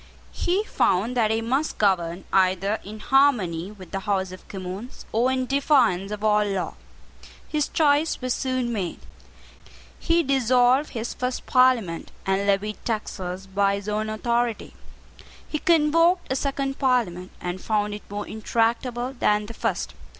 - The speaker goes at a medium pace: Yes, average, 150 wpm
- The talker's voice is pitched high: Yes, high, 220 Hz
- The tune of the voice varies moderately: Yes, average, 4.8 semitones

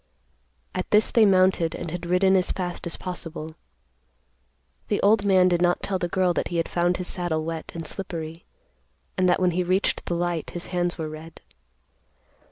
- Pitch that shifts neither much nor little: No, narrow, 1.7 semitones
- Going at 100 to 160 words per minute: No, average, 185 wpm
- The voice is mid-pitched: Yes, medium, 175 Hz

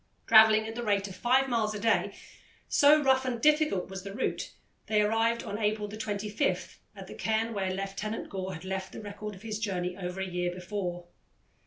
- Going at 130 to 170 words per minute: No, average, 195 wpm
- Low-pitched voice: No, high, 210 Hz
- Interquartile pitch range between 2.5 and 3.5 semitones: Yes, average, 2.8 semitones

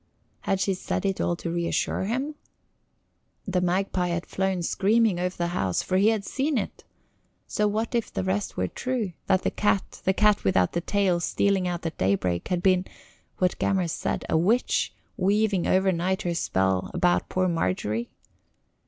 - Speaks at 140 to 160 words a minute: No, average, 170 wpm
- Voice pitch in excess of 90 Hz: Yes, medium, 185 Hz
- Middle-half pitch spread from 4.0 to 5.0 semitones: No, average, 2.8 semitones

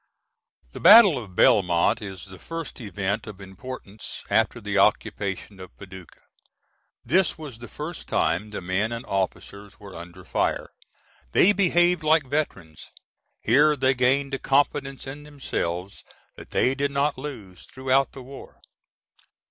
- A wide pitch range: Yes, wide, 6.7 semitones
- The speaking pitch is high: No, low, 125 Hz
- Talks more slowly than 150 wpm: Yes, average, 140 wpm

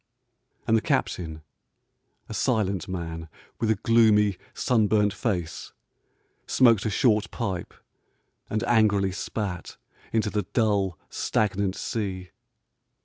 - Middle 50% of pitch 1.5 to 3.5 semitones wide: Yes, average, 2.9 semitones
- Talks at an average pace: No, slow, 105 wpm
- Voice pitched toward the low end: Yes, low, 105 Hz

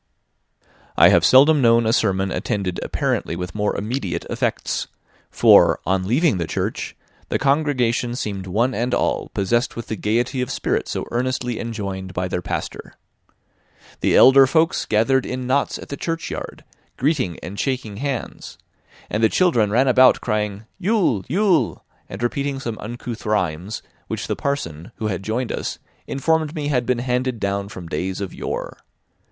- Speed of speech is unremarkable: Yes, average, 160 wpm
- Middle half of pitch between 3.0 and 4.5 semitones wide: No, average, 5.0 semitones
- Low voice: Yes, low, 115 Hz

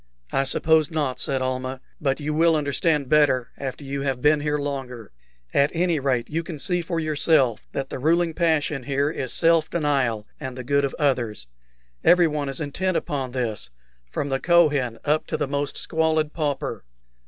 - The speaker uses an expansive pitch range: No, average, 3.1 semitones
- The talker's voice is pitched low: No, medium, 145 Hz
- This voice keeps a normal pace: Yes, average, 175 wpm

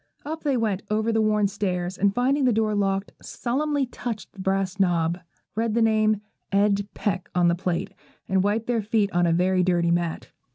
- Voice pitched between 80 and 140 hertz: No, high, 205 Hz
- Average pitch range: Yes, average, 3.3 semitones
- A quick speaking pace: No, average, 195 wpm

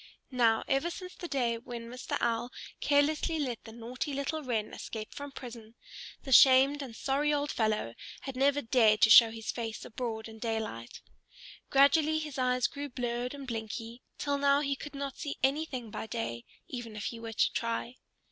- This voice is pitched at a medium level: No, very high, 250 Hz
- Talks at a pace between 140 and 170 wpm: No, average, 180 wpm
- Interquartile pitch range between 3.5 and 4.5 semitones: Yes, average, 3.8 semitones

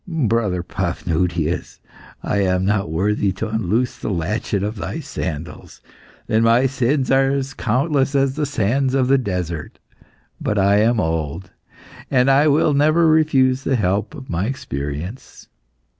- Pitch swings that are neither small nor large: No, wide, 6.6 semitones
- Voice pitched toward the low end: Yes, low, 110 Hz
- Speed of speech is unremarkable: Yes, average, 145 wpm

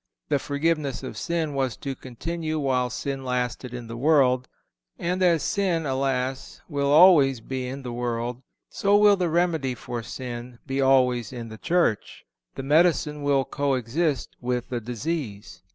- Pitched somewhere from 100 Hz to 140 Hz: Yes, low, 135 Hz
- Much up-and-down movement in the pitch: No, average, 4.1 semitones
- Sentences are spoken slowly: No, average, 160 wpm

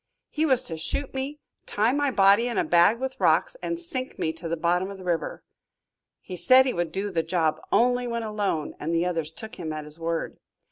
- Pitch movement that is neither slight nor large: No, wide, 7.0 semitones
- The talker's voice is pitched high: Yes, high, 195 Hz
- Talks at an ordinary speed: No, fast, 225 wpm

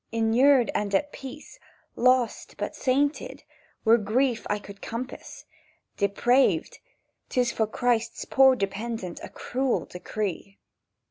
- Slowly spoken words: Yes, slow, 110 wpm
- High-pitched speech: Yes, high, 235 Hz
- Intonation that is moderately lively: Yes, average, 3.7 semitones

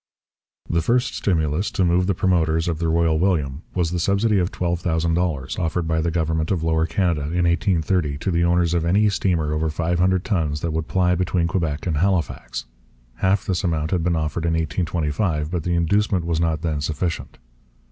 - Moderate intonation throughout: No, narrow, 2.1 semitones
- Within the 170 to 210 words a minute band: Yes, average, 190 wpm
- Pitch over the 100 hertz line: No, very low, 85 Hz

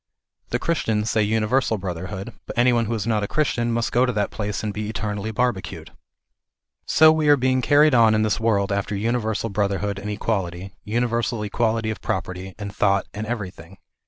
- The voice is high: No, low, 110 Hz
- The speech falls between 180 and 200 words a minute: Yes, average, 190 wpm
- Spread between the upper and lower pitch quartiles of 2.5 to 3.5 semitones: Yes, average, 2.8 semitones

